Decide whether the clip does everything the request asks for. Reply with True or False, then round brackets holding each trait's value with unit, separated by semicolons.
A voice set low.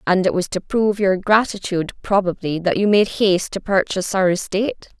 False (190 Hz)